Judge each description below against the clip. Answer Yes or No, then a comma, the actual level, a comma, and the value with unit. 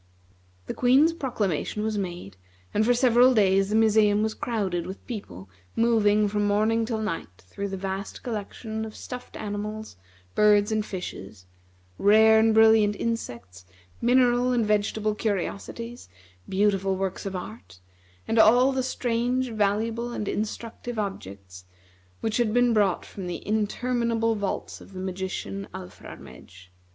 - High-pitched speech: Yes, high, 210 Hz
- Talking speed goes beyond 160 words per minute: No, average, 140 wpm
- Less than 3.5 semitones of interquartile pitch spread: Yes, average, 3.0 semitones